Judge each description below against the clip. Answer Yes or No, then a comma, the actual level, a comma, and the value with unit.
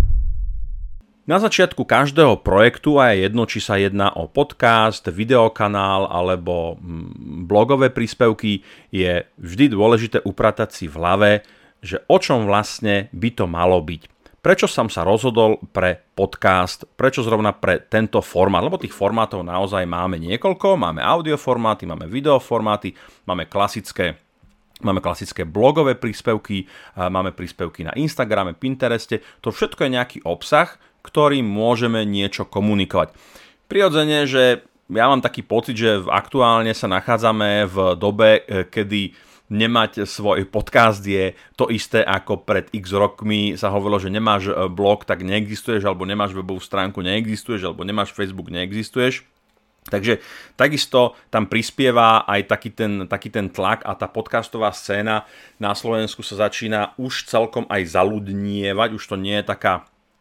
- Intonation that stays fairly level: No, average, 3.0 semitones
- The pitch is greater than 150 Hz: No, low, 105 Hz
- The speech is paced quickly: No, average, 140 wpm